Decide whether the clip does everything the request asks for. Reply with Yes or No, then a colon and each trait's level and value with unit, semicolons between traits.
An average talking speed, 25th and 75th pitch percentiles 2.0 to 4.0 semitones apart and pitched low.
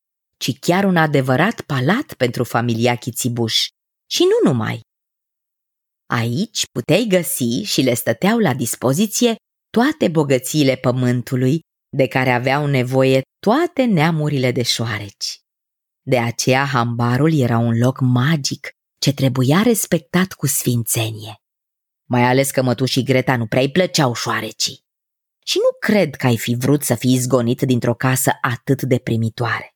No: average, 135 wpm; average, 4.4 semitones; low, 130 Hz